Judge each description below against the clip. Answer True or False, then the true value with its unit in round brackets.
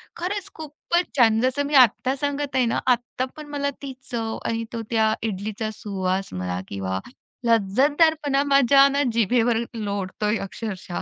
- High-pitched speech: True (235 Hz)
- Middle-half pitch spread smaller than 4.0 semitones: False (5.2 semitones)